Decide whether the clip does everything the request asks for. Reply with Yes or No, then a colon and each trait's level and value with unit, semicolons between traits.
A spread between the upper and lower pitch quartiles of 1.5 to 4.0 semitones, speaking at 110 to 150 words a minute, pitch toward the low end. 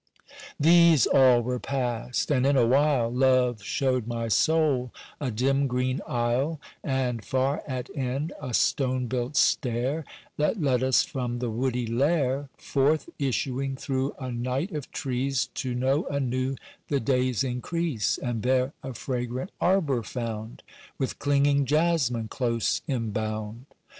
Yes: narrow, 2.4 semitones; average, 140 wpm; low, 130 Hz